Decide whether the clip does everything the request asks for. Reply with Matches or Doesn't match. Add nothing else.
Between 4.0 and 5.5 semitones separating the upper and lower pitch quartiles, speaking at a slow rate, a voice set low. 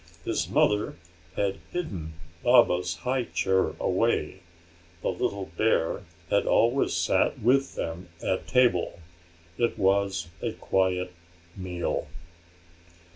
Matches